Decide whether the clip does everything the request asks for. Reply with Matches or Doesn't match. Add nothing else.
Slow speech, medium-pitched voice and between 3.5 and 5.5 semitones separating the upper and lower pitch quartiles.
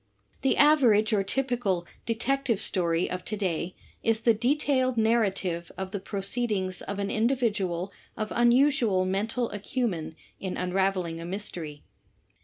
Doesn't match